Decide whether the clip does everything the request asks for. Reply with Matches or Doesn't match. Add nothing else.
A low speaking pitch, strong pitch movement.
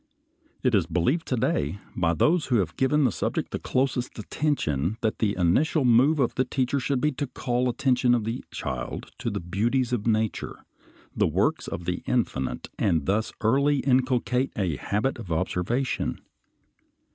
Matches